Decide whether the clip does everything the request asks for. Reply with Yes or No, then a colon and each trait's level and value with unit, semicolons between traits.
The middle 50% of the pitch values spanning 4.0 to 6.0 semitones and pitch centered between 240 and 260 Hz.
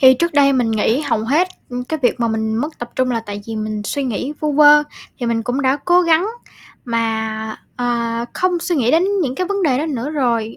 Yes: average, 4.7 semitones; very high, 255 Hz